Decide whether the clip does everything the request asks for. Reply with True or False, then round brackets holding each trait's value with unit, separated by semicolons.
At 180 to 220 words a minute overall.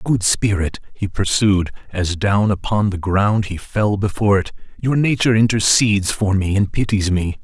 False (170 wpm)